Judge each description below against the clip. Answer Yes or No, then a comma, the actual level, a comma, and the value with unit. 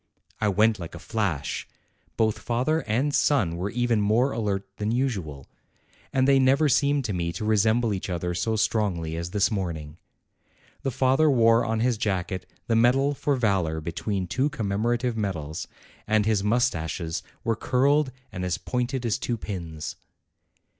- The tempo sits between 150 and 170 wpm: Yes, average, 160 wpm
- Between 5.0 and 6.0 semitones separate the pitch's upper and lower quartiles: Yes, average, 5.3 semitones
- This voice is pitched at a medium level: No, low, 110 Hz